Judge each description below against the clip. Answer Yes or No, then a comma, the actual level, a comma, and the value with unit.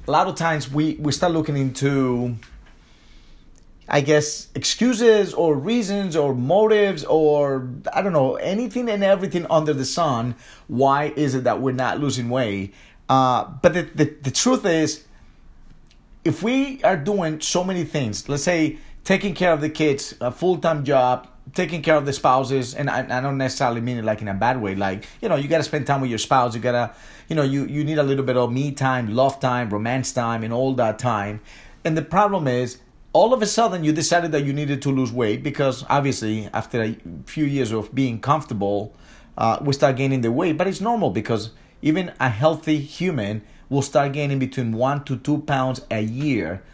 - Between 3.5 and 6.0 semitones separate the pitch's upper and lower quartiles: Yes, average, 4.3 semitones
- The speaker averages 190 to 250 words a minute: Yes, average, 200 wpm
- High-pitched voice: No, medium, 140 Hz